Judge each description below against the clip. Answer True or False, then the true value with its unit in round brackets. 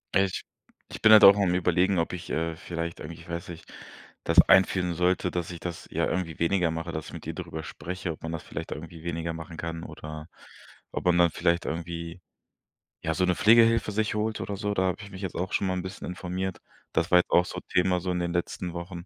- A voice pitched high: False (90 Hz)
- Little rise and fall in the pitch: True (2.1 semitones)